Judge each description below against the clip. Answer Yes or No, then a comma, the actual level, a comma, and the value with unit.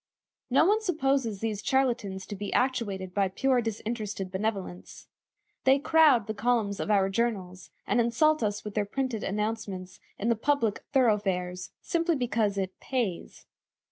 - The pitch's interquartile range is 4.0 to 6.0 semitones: Yes, average, 4.6 semitones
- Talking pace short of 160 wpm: Yes, average, 145 wpm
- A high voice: Yes, high, 220 Hz